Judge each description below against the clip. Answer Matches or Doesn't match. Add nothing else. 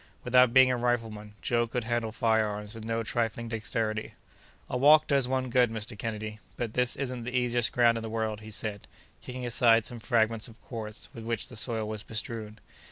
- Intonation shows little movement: Matches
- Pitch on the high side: Doesn't match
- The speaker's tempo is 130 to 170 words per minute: Doesn't match